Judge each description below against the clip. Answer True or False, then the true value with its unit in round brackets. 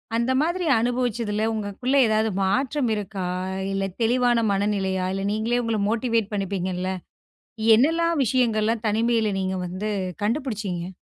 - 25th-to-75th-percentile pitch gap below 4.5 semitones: True (3.7 semitones)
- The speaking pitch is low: False (220 Hz)